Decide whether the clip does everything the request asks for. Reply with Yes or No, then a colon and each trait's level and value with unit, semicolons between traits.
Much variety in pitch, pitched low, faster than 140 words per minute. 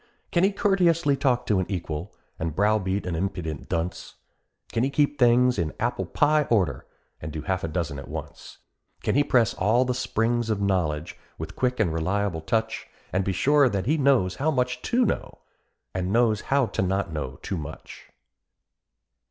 Yes: wide, 6.4 semitones; low, 105 Hz; average, 180 wpm